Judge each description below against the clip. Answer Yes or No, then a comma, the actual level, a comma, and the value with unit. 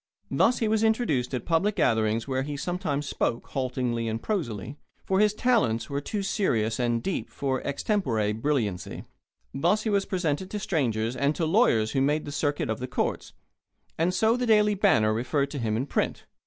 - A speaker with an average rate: Yes, average, 190 wpm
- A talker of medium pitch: Yes, medium, 145 Hz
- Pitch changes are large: Yes, wide, 8.8 semitones